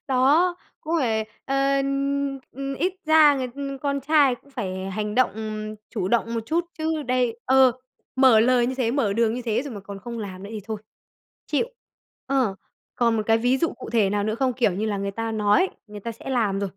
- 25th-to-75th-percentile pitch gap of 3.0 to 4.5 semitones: Yes, average, 4.2 semitones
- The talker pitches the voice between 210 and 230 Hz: No, high, 240 Hz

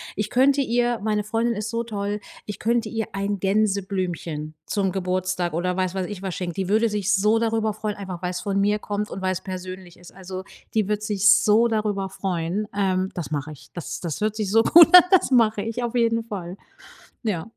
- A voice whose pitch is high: Yes, high, 205 Hz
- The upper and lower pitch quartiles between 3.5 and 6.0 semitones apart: No, average, 2.9 semitones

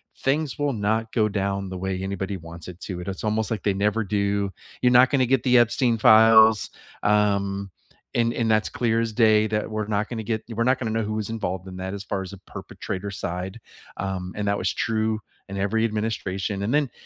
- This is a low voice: Yes, low, 105 Hz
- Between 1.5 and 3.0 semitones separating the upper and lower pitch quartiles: Yes, narrow, 2.5 semitones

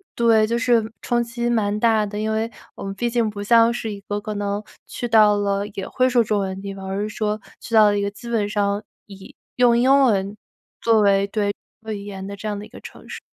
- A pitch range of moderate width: No, narrow, 2.3 semitones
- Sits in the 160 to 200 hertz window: No, high, 210 Hz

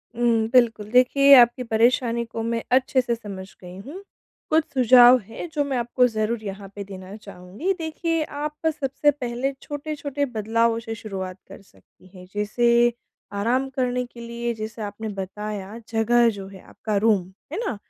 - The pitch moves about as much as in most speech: Yes, average, 3.5 semitones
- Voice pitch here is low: No, high, 235 Hz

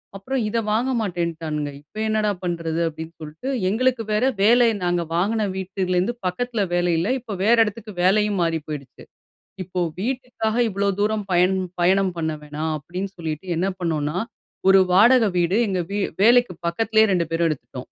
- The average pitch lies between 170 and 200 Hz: Yes, high, 190 Hz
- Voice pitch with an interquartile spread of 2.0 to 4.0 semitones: No, average, 4.5 semitones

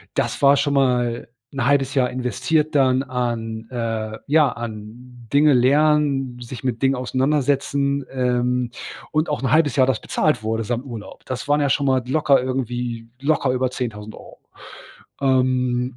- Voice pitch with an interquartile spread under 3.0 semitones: Yes, narrow, 2.4 semitones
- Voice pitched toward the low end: Yes, low, 130 Hz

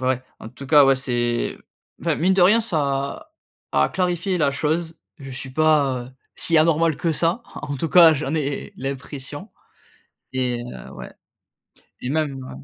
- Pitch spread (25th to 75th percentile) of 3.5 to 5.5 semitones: Yes, average, 3.9 semitones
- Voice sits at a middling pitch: Yes, medium, 145 Hz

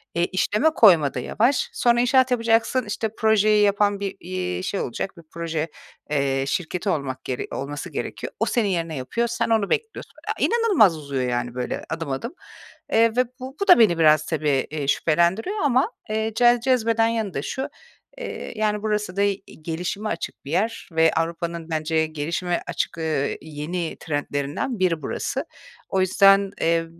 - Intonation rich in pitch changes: Yes, wide, 6.1 semitones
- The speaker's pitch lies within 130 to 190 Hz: Yes, medium, 185 Hz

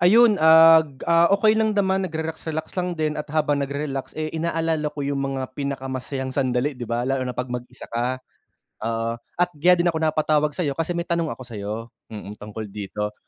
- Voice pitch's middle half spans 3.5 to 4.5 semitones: Yes, average, 4.2 semitones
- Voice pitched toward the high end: No, medium, 150 Hz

